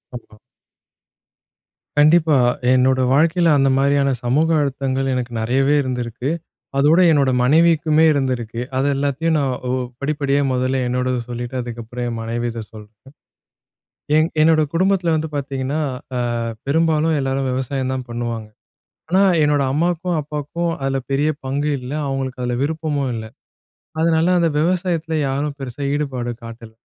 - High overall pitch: No, low, 135 Hz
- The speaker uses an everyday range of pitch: Yes, average, 3.6 semitones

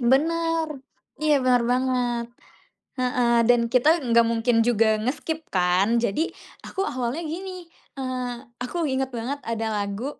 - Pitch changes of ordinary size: Yes, average, 4.3 semitones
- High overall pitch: Yes, very high, 250 Hz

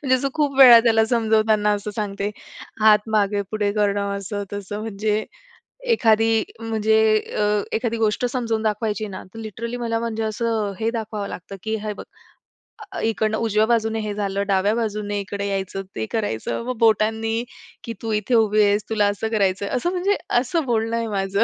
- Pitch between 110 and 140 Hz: No, high, 220 Hz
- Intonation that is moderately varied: No, narrow, 1.8 semitones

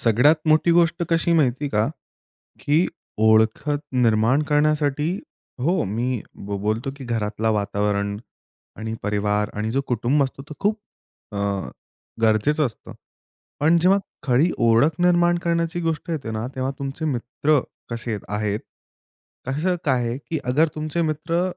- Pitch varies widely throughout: Yes, wide, 6.1 semitones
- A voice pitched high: No, low, 135 Hz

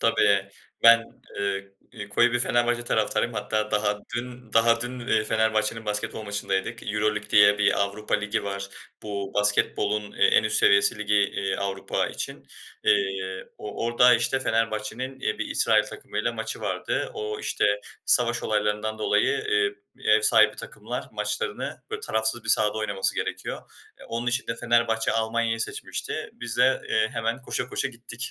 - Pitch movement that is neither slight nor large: No, narrow, 2.3 semitones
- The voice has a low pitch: Yes, low, 110 Hz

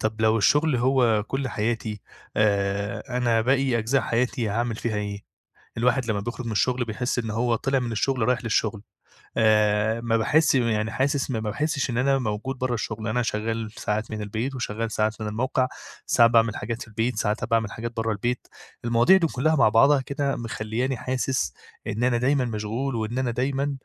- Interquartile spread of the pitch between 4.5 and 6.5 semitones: No, average, 2.9 semitones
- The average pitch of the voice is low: Yes, low, 115 Hz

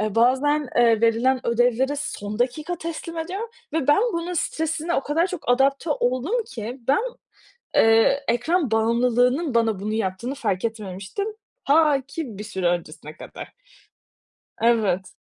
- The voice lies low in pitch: No, very high, 250 Hz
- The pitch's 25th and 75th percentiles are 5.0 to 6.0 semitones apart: Yes, average, 5.3 semitones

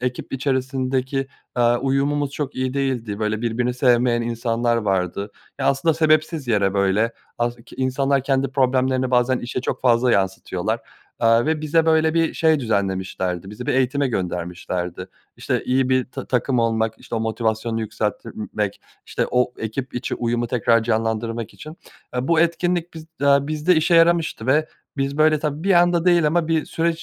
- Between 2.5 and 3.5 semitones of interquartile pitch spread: No, average, 4.3 semitones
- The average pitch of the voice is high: No, low, 125 Hz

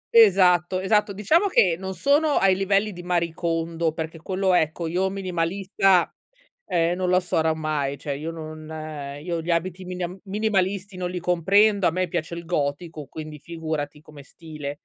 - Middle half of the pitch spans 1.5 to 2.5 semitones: No, average, 2.9 semitones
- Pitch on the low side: No, medium, 175 Hz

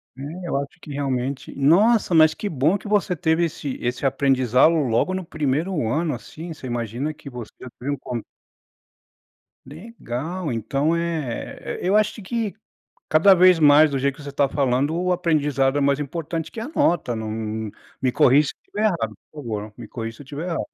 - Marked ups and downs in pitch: No, average, 4.7 semitones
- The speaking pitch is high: No, medium, 145 Hz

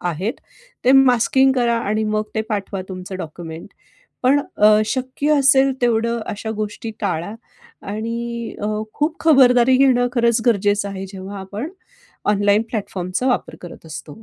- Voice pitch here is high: Yes, high, 220 Hz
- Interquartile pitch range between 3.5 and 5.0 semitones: Yes, average, 3.9 semitones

